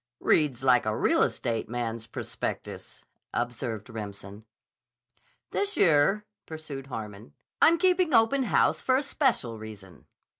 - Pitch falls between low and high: No, low, 125 Hz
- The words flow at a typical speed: No, slow, 120 wpm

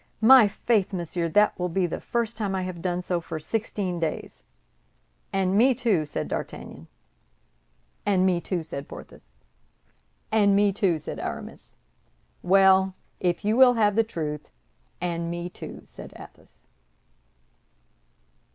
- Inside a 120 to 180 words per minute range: Yes, average, 140 wpm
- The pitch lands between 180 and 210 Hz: Yes, high, 190 Hz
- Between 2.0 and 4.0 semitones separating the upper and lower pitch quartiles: Yes, average, 3.3 semitones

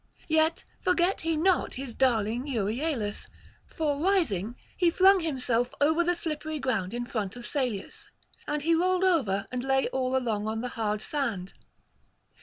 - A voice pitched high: Yes, very high, 270 Hz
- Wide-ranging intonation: Yes, wide, 6.3 semitones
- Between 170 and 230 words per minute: No, average, 155 wpm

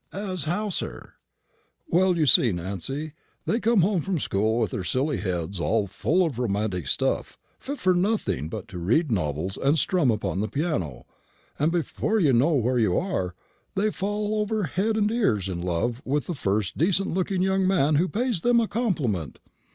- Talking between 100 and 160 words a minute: No, average, 180 wpm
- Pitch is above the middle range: No, medium, 150 Hz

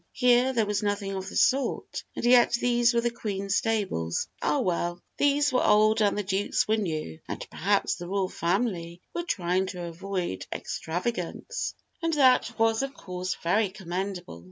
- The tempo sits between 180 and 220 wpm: No, average, 170 wpm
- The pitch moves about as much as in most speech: Yes, average, 4.9 semitones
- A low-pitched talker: No, high, 200 Hz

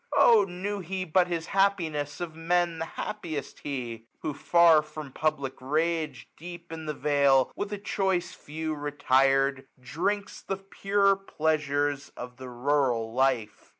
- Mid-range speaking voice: Yes, medium, 155 Hz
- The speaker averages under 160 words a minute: Yes, average, 150 wpm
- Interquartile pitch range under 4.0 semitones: No, average, 4.4 semitones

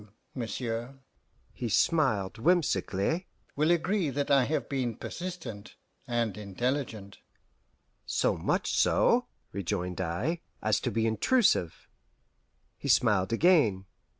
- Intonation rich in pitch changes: Yes, wide, 7.0 semitones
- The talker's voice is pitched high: No, low, 120 Hz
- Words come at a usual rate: No, slow, 110 wpm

